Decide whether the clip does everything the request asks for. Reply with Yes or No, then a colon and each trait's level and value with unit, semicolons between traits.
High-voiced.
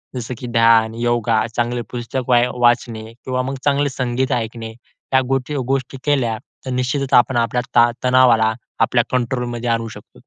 No: low, 120 Hz